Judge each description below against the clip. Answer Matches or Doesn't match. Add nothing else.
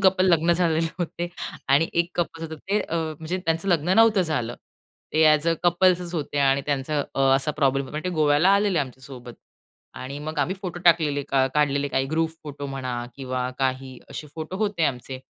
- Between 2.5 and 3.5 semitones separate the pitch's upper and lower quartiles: Doesn't match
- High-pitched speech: Doesn't match